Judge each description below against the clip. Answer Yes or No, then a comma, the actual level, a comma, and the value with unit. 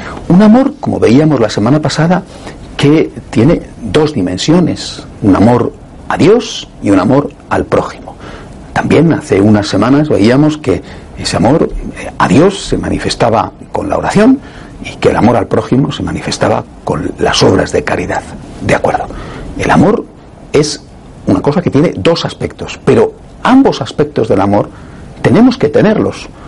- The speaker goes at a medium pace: Yes, average, 150 wpm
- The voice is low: No, medium, 150 Hz